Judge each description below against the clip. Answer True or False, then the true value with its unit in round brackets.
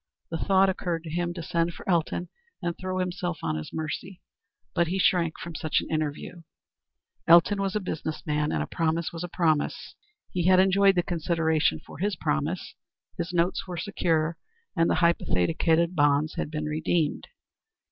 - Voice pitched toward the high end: False (170 Hz)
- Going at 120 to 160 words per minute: False (175 wpm)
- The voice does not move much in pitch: True (2.3 semitones)